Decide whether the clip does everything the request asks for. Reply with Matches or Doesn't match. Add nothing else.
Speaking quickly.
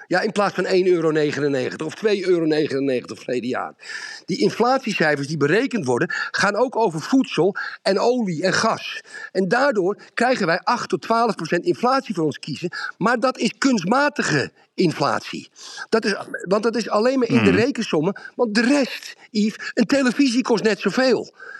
Doesn't match